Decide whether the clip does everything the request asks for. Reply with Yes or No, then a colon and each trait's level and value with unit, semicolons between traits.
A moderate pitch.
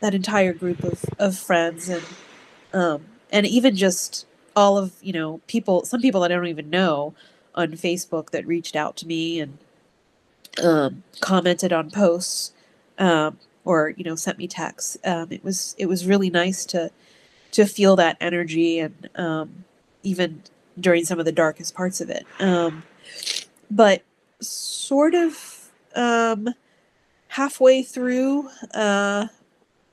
Yes: medium, 180 Hz